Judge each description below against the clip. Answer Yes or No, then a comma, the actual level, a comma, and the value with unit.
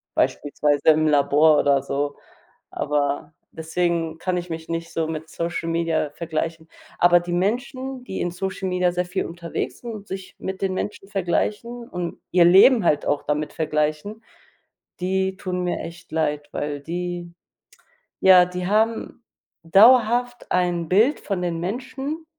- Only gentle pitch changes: No, average, 3.3 semitones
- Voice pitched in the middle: Yes, medium, 175 Hz